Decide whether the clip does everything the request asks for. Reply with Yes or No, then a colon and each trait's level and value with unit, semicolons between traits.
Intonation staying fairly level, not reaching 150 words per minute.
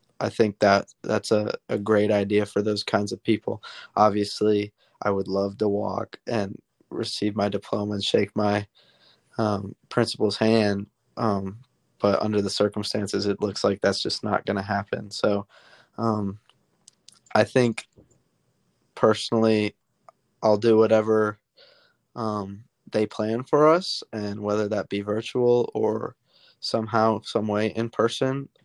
Yes: narrow, 1.6 semitones; average, 140 wpm